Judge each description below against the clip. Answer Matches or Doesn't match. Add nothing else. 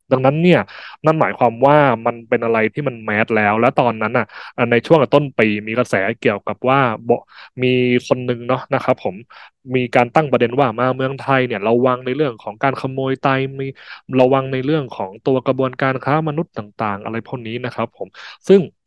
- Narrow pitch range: Matches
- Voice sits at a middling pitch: Doesn't match